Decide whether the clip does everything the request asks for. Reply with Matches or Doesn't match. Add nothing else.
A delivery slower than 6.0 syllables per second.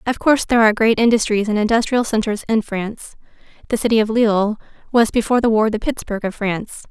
Doesn't match